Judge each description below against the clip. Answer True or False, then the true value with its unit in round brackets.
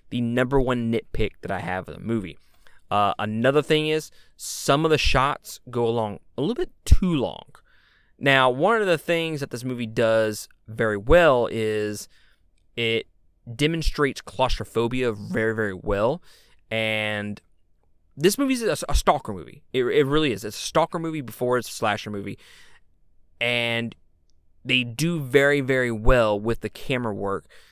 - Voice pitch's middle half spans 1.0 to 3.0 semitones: False (4.7 semitones)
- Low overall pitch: True (115 Hz)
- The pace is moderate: True (160 wpm)